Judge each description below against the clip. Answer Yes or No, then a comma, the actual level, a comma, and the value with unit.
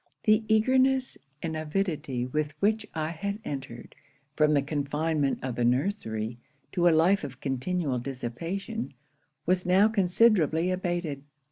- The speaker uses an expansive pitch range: Yes, wide, 6.0 semitones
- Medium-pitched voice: Yes, medium, 160 Hz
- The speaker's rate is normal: No, slow, 130 wpm